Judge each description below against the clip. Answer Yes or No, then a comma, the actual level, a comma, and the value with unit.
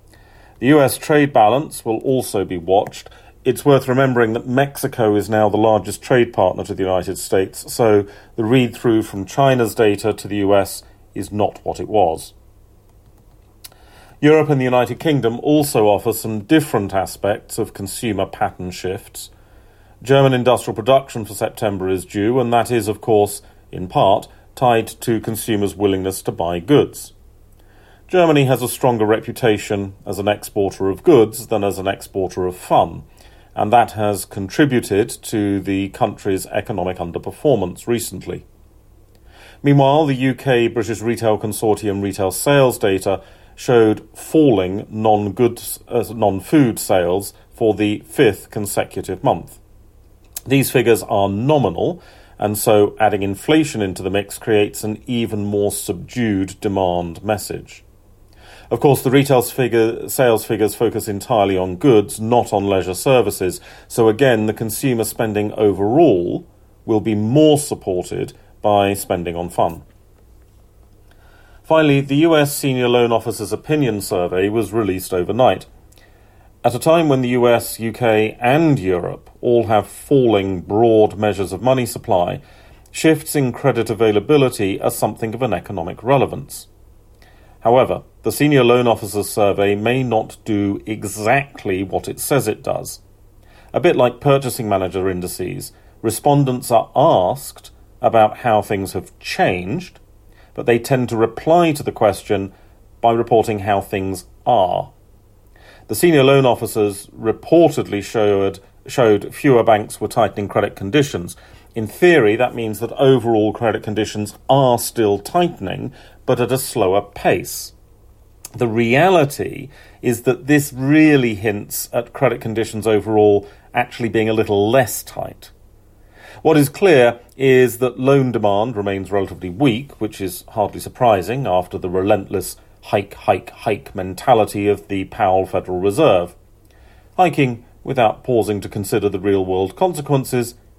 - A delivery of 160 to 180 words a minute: No, average, 140 wpm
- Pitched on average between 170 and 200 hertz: No, low, 105 Hz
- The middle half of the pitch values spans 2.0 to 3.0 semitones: No, average, 3.4 semitones